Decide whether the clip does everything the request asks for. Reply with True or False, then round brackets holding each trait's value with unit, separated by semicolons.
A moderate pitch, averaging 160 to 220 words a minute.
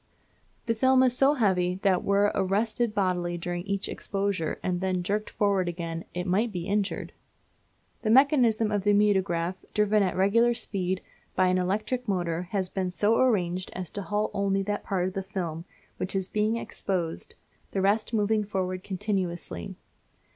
False (195 Hz; 170 wpm)